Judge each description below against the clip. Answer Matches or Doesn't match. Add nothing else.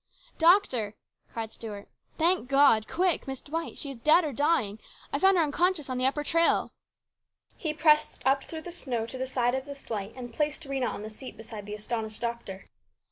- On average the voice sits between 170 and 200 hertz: Doesn't match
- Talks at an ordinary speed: Doesn't match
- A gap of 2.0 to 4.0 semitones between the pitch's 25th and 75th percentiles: Doesn't match